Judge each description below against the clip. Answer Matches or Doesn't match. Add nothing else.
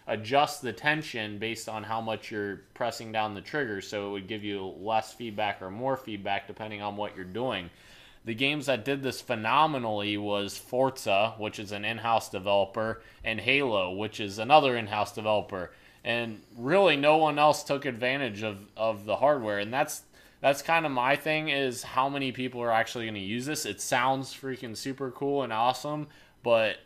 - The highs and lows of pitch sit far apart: Doesn't match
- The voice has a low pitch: Matches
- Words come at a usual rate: Matches